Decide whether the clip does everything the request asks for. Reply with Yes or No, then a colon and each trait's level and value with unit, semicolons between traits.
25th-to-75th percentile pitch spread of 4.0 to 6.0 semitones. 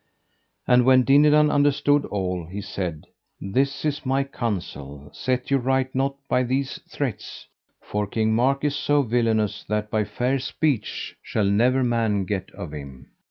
Yes: average, 5.1 semitones